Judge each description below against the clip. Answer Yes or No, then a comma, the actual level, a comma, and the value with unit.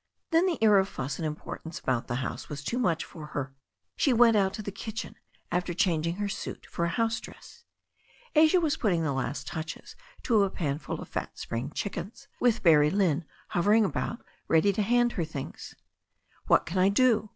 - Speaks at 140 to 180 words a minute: No, average, 195 wpm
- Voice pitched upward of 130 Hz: Yes, high, 190 Hz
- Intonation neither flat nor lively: No, wide, 6.3 semitones